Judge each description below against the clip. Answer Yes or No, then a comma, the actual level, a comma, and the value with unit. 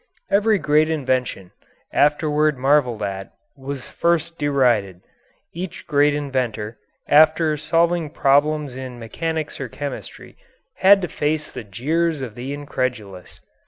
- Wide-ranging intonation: No, average, 3.8 semitones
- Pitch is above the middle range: No, medium, 145 Hz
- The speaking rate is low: Yes, slow, 120 wpm